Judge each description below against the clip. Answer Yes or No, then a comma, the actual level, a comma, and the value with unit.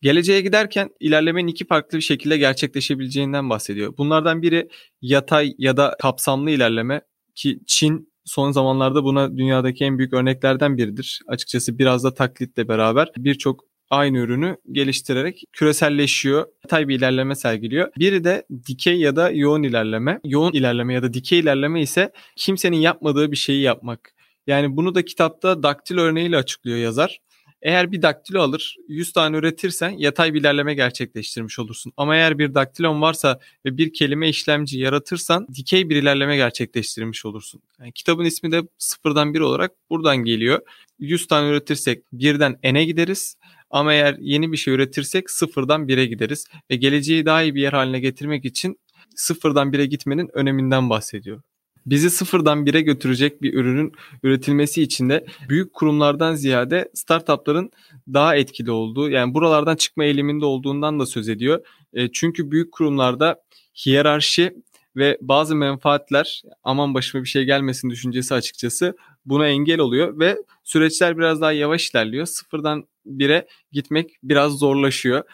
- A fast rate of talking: Yes, fast, 145 wpm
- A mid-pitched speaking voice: Yes, medium, 145 Hz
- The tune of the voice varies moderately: Yes, average, 3.3 semitones